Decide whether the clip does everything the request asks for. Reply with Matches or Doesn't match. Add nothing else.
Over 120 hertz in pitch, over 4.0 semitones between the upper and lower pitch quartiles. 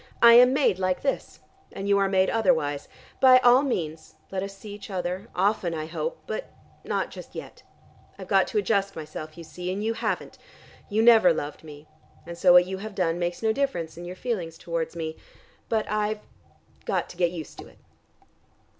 Matches